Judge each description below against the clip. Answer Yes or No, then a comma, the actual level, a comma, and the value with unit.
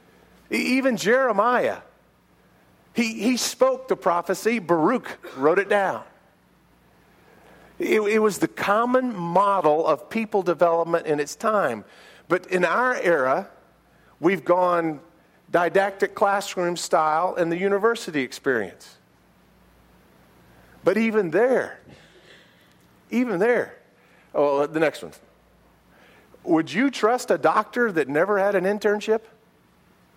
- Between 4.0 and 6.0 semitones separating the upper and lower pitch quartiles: Yes, average, 5.1 semitones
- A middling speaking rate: No, slow, 110 wpm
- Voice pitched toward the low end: No, high, 200 Hz